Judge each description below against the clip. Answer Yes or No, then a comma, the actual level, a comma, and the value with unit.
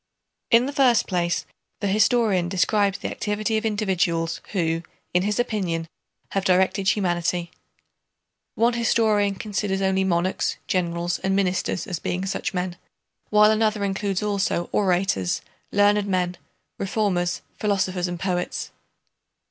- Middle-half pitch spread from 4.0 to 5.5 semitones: No, average, 2.8 semitones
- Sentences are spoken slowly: Yes, slow, 125 wpm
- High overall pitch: Yes, high, 195 Hz